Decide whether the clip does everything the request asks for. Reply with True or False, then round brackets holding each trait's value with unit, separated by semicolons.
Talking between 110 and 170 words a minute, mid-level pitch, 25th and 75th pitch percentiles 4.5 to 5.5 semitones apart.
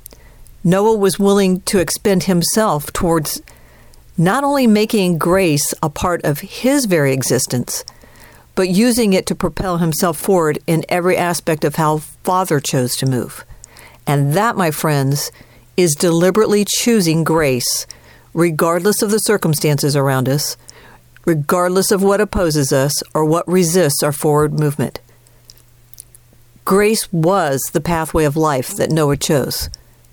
True (135 wpm; 165 Hz; 5.2 semitones)